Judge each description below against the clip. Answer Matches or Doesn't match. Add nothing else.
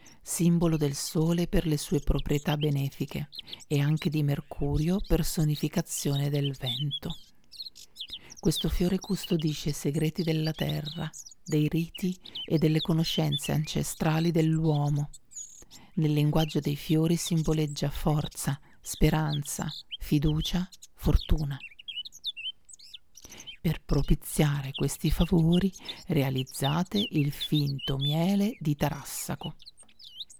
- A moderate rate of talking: Doesn't match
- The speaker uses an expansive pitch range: Doesn't match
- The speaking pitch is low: Doesn't match